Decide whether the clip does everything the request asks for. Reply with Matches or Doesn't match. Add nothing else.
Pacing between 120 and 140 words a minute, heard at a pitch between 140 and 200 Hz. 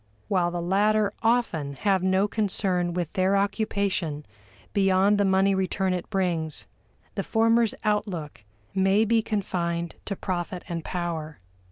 Matches